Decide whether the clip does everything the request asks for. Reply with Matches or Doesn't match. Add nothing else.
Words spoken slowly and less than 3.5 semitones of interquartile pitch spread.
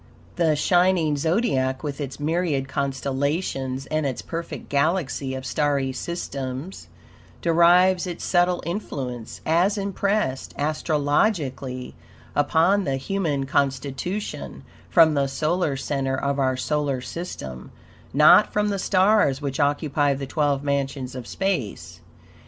Doesn't match